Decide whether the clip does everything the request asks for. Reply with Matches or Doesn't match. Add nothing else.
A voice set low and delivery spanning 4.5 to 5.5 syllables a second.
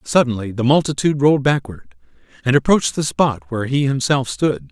Doesn't match